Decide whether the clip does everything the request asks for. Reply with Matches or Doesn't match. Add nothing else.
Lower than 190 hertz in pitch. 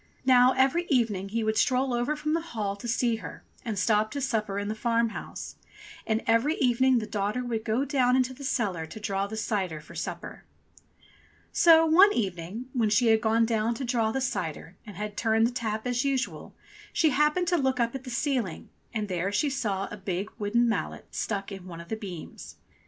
Doesn't match